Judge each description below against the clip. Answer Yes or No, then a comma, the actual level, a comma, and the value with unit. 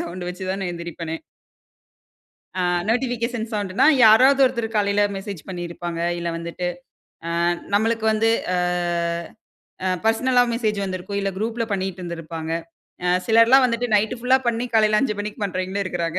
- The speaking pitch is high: Yes, high, 205 Hz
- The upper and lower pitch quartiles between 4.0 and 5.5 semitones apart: Yes, average, 4.3 semitones